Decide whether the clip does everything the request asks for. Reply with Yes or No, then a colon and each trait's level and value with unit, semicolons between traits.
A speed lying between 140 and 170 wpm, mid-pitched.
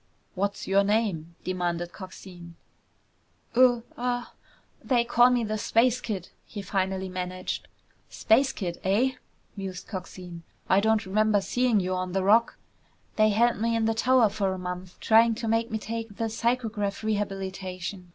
No: average, 150 wpm; high, 205 Hz